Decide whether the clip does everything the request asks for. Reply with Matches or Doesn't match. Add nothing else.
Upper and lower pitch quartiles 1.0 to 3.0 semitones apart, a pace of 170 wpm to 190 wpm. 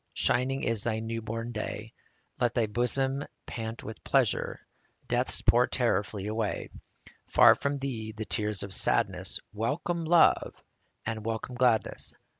Doesn't match